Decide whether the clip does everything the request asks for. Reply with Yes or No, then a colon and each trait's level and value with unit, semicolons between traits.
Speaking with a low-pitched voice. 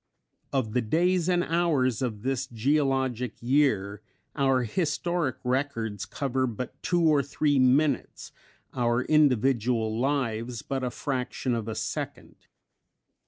Yes: low, 130 Hz